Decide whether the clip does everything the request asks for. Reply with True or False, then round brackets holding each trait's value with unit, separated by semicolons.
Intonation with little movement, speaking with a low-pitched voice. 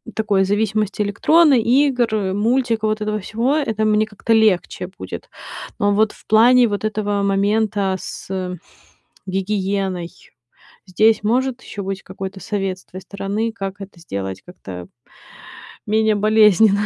False (2.3 semitones; 210 Hz)